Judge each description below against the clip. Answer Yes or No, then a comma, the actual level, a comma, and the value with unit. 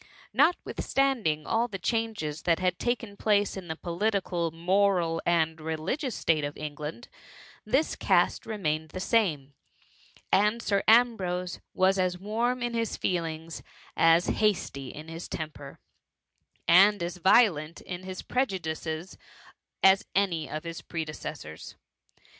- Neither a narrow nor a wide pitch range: Yes, average, 4.7 semitones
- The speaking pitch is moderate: Yes, medium, 180 Hz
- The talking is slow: Yes, slow, 125 wpm